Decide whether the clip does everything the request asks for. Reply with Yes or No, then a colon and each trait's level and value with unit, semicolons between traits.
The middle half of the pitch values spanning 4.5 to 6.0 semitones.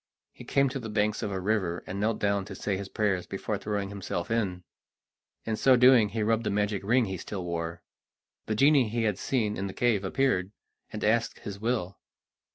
No: average, 2.7 semitones